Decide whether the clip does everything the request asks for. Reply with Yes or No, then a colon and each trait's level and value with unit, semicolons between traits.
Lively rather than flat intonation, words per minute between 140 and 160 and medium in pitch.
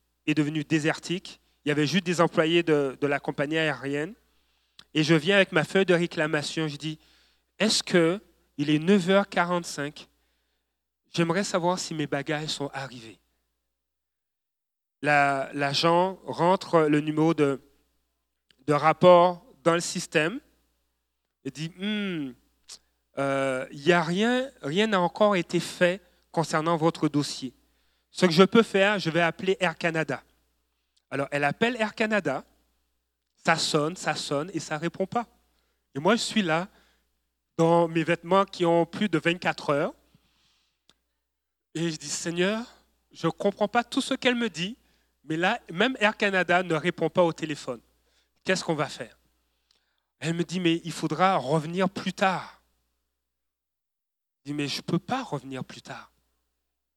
Yes: wide, 8.3 semitones; average, 155 wpm; medium, 155 Hz